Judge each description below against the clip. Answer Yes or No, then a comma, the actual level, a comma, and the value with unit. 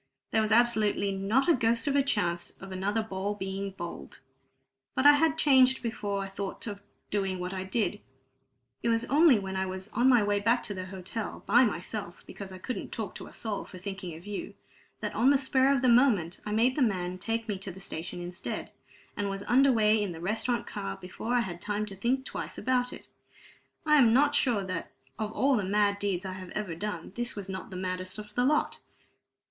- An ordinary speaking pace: No, fast, 220 wpm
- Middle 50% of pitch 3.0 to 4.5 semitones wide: Yes, average, 4.1 semitones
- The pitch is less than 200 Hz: No, high, 205 Hz